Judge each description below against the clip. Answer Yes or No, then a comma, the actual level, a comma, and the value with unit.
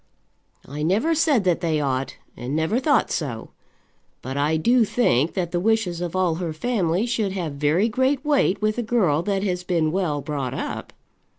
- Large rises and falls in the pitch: Yes, wide, 6.3 semitones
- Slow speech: No, average, 185 wpm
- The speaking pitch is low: No, medium, 180 Hz